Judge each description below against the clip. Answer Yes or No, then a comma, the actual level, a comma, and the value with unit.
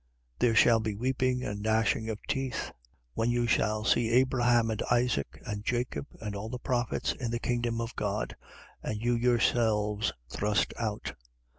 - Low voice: Yes, low, 115 Hz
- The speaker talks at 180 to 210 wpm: No, average, 165 wpm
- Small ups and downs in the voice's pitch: Yes, narrow, 2.2 semitones